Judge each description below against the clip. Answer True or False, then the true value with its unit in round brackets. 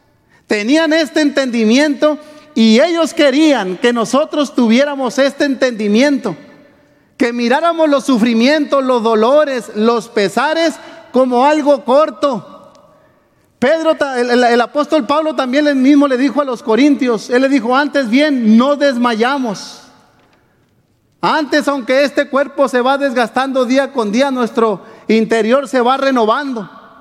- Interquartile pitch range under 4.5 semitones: True (3.7 semitones)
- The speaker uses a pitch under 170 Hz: False (270 Hz)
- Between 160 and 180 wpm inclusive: False (130 wpm)